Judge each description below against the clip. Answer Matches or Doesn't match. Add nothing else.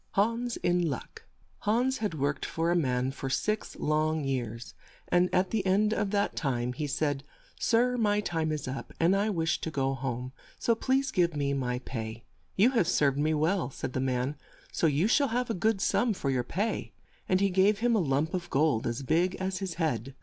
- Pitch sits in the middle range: Matches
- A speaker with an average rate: Doesn't match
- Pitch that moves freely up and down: Matches